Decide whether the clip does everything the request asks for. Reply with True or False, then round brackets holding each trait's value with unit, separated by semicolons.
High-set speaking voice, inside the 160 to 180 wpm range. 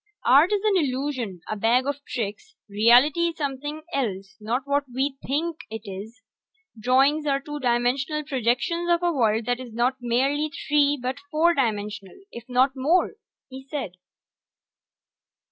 False (265 Hz; 150 wpm)